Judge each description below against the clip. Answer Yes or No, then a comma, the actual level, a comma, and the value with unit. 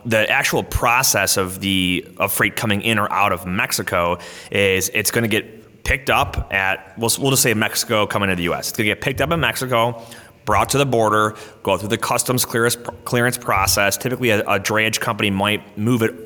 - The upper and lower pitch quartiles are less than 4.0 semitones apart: Yes, average, 2.9 semitones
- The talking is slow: No, fast, 205 wpm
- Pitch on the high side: No, low, 110 Hz